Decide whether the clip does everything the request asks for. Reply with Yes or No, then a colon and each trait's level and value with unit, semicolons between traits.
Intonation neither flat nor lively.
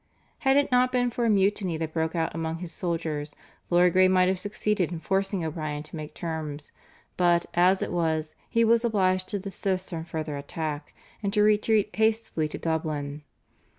Yes: average, 4.2 semitones